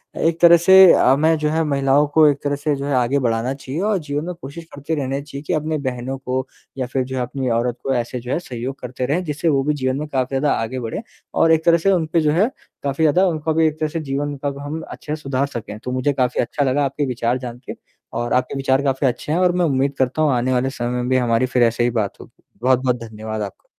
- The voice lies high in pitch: No, low, 135 Hz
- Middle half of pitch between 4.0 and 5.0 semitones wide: No, average, 3.3 semitones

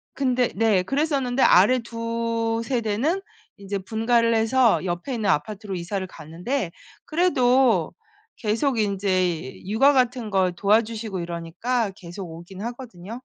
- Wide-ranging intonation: No, average, 4.7 semitones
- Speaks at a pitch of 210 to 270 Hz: Yes, high, 225 Hz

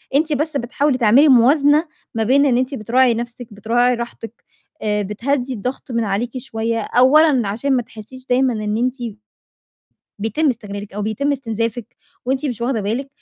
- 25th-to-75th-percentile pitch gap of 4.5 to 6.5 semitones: No, average, 3.3 semitones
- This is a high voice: Yes, high, 245 Hz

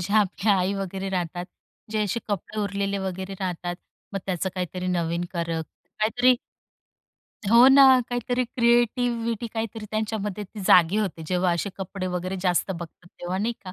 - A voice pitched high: Yes, high, 195 Hz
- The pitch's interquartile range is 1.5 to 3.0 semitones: No, average, 3.5 semitones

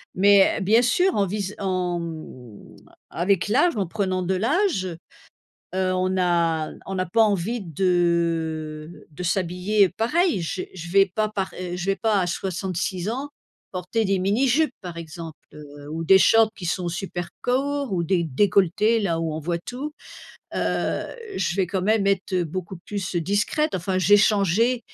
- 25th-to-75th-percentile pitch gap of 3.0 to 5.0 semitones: Yes, average, 3.6 semitones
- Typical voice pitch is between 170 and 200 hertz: Yes, medium, 185 Hz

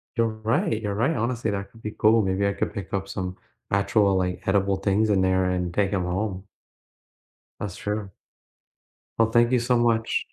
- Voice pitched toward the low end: Yes, low, 100 Hz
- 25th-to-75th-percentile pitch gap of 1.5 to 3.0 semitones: Yes, average, 2.7 semitones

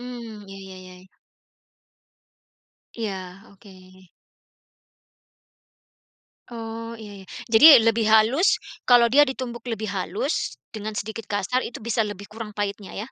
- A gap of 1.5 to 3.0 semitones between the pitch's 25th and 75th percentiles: Yes, narrow, 2.4 semitones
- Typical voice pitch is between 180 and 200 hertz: No, high, 220 Hz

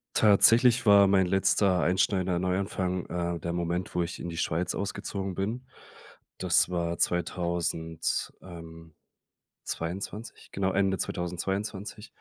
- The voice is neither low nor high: No, very low, 90 Hz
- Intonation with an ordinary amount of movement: No, narrow, 2.2 semitones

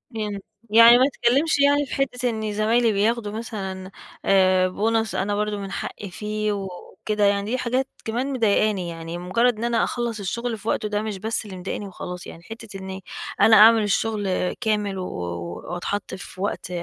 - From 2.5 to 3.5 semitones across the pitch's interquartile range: Yes, average, 3.1 semitones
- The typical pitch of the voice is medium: No, high, 210 Hz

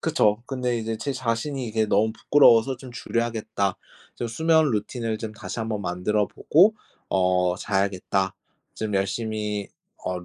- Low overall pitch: Yes, low, 110 Hz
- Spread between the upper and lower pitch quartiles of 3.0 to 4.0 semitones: Yes, average, 3.3 semitones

